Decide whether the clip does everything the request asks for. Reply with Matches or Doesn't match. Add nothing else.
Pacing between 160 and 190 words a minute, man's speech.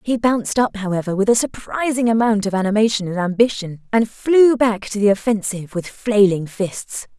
Doesn't match